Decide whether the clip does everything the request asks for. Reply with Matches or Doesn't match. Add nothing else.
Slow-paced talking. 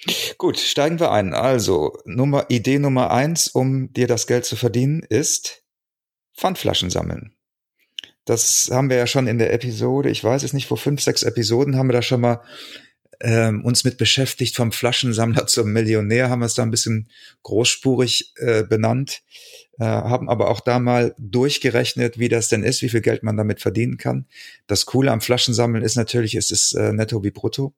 Doesn't match